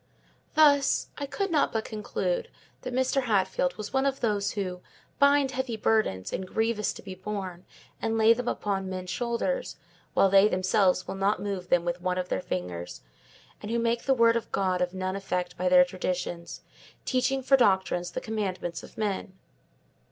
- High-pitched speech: Yes, high, 205 Hz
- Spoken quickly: No, average, 180 wpm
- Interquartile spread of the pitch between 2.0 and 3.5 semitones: No, average, 4.5 semitones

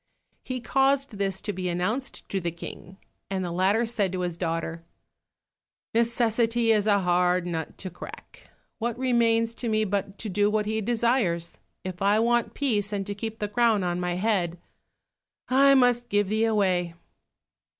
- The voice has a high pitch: Yes, high, 205 Hz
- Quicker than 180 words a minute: No, average, 170 wpm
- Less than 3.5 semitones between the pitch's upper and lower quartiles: No, average, 4.2 semitones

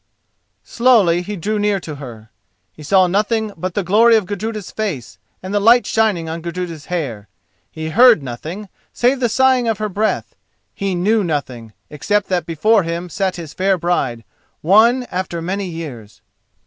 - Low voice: No, medium, 185 Hz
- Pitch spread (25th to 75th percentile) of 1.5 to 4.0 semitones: No, average, 4.8 semitones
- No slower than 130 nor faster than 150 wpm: No, average, 170 wpm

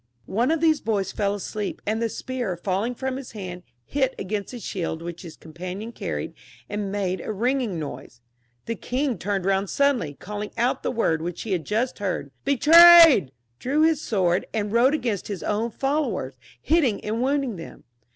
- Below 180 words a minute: No, average, 190 wpm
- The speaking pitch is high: Yes, high, 210 Hz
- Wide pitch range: Yes, wide, 5.8 semitones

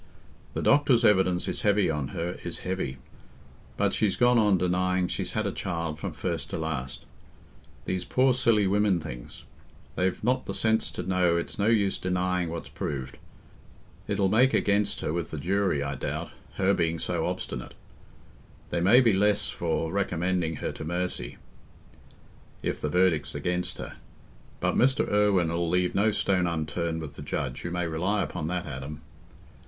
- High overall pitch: No, very low, 90 Hz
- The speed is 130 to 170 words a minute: Yes, average, 160 wpm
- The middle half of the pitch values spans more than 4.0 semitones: No, average, 3.7 semitones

